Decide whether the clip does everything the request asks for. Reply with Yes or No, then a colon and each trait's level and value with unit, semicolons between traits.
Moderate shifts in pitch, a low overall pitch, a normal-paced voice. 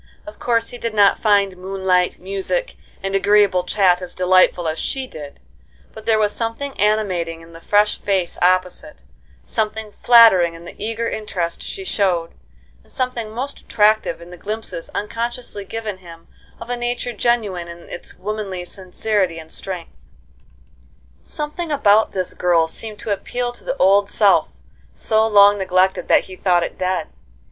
No: average, 3.6 semitones; high, 200 Hz; average, 160 wpm